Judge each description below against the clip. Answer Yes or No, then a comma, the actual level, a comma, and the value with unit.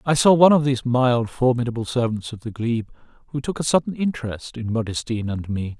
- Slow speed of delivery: No, fast, 205 wpm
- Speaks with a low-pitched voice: Yes, low, 125 Hz